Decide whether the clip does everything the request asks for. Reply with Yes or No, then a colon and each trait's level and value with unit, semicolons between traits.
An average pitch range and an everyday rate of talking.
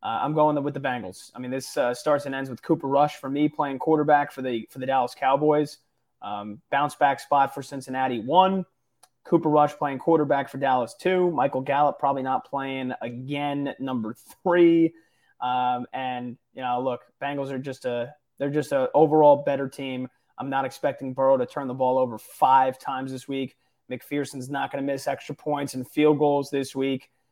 No: narrow, 2.2 semitones; average, 195 wpm